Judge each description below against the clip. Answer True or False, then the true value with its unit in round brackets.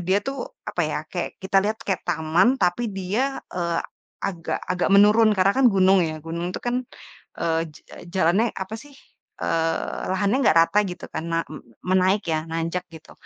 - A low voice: False (185 Hz)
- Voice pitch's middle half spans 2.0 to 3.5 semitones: False (3.9 semitones)